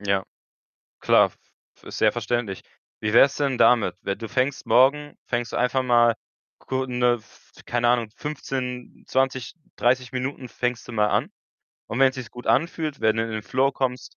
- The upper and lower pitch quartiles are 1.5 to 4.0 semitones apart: Yes, narrow, 2.4 semitones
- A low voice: Yes, low, 125 Hz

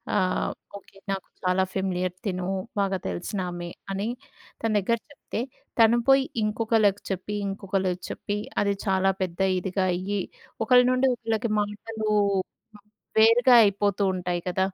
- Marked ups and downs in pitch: No, average, 2.8 semitones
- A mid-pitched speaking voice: No, high, 195 Hz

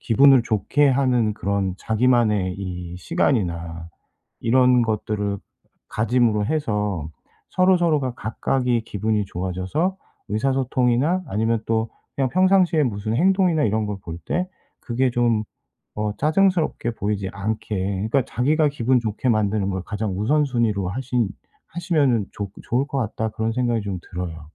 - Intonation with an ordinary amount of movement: Yes, average, 4.7 semitones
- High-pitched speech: No, low, 115 Hz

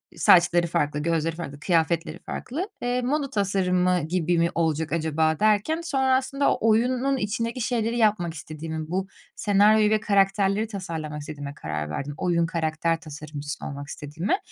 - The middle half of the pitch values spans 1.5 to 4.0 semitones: No, wide, 5.4 semitones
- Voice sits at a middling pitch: Yes, medium, 175 Hz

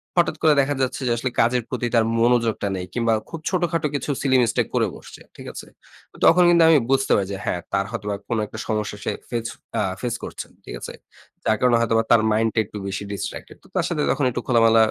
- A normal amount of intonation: Yes, average, 3.5 semitones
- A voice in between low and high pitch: No, low, 115 Hz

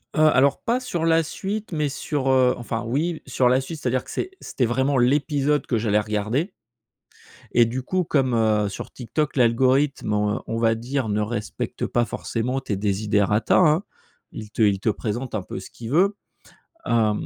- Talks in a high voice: No, low, 125 Hz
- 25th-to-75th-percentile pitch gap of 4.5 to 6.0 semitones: Yes, average, 5.1 semitones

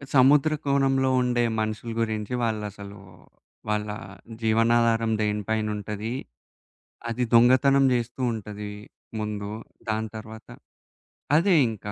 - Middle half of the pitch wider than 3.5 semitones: No, average, 2.7 semitones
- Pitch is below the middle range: Yes, low, 110 Hz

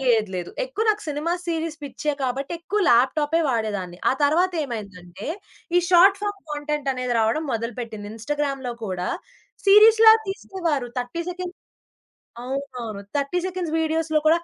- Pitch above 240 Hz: Yes, very high, 290 Hz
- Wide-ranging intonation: Yes, wide, 6.7 semitones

